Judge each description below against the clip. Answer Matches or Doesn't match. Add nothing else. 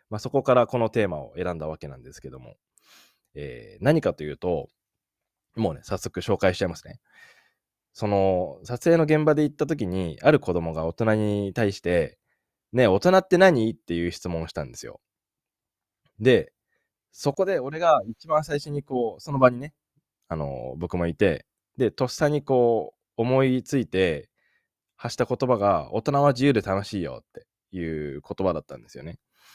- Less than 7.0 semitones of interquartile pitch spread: Doesn't match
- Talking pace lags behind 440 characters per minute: Matches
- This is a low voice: Matches